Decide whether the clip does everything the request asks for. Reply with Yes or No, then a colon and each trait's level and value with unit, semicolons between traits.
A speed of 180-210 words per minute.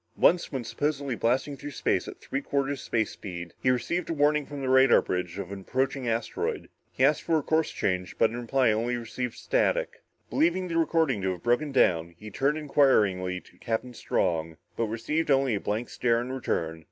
Yes: average, 200 wpm